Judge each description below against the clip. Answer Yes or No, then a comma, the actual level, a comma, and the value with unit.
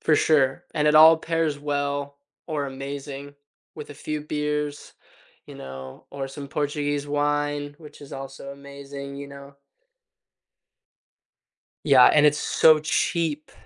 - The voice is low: No, medium, 145 Hz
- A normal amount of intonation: No, narrow, 1.2 semitones